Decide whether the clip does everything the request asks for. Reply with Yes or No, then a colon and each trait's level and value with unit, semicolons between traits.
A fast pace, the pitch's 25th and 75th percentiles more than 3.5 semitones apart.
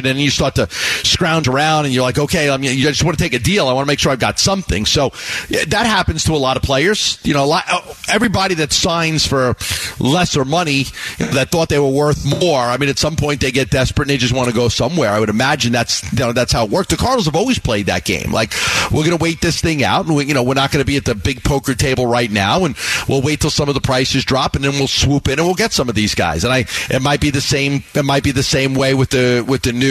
No: fast, 295 wpm; average, 3.1 semitones